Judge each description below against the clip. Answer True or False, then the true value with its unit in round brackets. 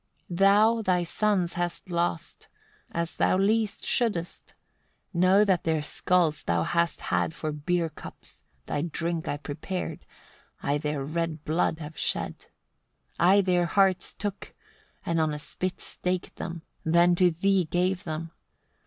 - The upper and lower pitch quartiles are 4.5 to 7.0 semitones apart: False (2.6 semitones)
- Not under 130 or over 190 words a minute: True (145 wpm)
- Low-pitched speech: False (175 Hz)